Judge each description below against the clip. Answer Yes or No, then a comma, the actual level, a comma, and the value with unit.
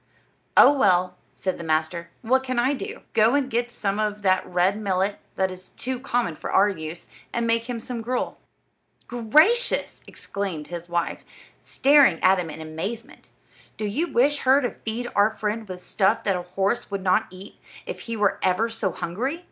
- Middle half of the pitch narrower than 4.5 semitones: No, average, 4.8 semitones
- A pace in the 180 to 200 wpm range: Yes, average, 185 wpm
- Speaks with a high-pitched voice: Yes, high, 210 Hz